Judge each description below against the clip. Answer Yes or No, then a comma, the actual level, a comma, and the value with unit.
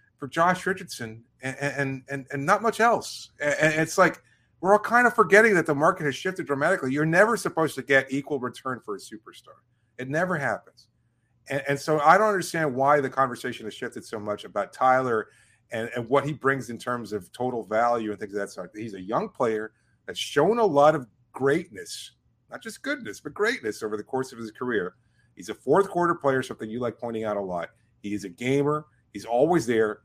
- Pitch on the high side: No, low, 135 Hz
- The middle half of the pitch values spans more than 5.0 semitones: Yes, wide, 5.4 semitones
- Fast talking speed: Yes, fast, 215 wpm